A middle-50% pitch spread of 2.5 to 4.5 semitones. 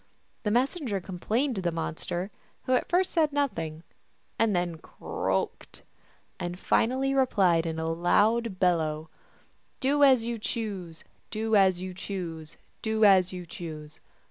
No: wide, 5.6 semitones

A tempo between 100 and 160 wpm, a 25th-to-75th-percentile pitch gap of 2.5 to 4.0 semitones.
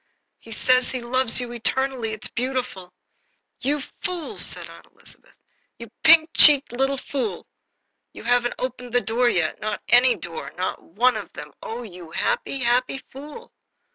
Yes: average, 155 wpm; average, 3.0 semitones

